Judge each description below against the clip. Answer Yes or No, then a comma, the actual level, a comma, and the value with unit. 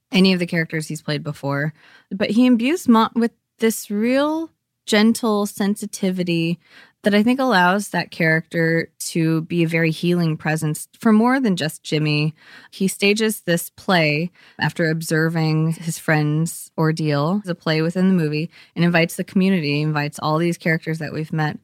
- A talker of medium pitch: Yes, medium, 170 Hz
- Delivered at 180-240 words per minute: No, average, 165 wpm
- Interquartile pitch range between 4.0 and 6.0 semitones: Yes, average, 4.6 semitones